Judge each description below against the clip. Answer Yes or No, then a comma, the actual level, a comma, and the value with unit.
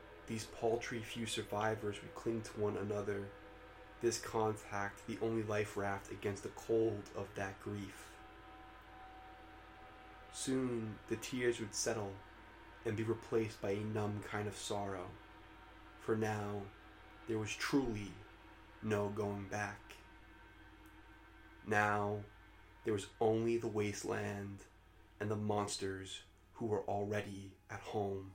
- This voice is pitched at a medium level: No, low, 105 Hz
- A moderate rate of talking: No, slow, 120 wpm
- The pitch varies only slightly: Yes, narrow, 1.5 semitones